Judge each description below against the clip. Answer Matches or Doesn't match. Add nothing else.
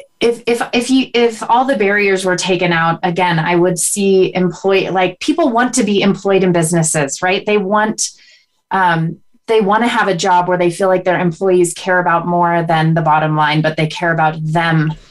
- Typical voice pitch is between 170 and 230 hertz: Matches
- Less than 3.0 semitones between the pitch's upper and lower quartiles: Doesn't match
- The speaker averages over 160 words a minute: Matches